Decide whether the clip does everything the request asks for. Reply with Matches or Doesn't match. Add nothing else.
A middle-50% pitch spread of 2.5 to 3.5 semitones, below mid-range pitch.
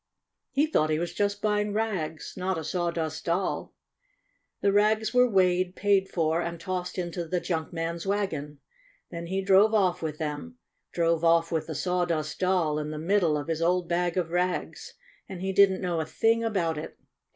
Doesn't match